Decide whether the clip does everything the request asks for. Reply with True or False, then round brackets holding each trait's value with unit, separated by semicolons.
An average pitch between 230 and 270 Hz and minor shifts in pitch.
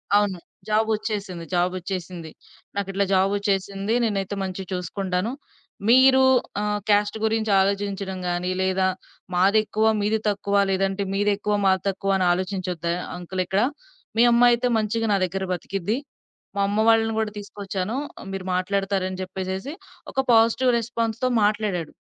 False (200 Hz; 2.3 semitones)